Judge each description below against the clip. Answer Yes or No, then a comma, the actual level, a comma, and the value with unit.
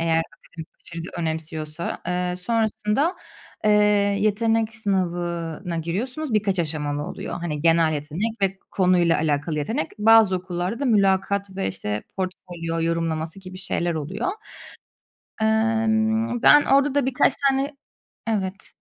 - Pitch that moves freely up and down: No, average, 4.9 semitones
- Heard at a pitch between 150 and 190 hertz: Yes, medium, 185 Hz